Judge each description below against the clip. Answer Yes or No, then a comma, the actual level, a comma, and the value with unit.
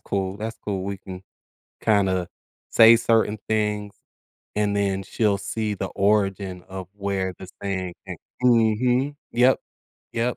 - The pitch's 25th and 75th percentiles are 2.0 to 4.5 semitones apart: Yes, narrow, 2.6 semitones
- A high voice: No, low, 100 Hz